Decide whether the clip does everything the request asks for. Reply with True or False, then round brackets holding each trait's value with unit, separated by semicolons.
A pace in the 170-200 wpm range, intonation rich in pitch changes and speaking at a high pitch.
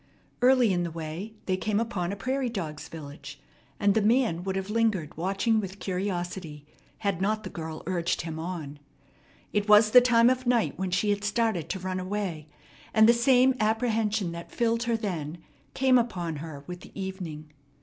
False (180 wpm; 4.8 semitones; 195 Hz)